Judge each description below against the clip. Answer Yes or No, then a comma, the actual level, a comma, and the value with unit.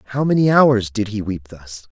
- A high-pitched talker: No, low, 110 Hz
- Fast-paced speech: Yes, fast, 215 wpm